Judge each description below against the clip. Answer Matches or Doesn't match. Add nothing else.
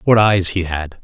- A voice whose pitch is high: Doesn't match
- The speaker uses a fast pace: Matches